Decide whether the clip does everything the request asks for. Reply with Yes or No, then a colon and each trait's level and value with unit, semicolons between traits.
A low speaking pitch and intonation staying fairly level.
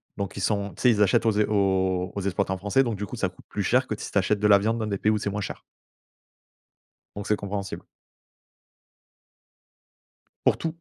Yes: low, 100 Hz; narrow, 1.6 semitones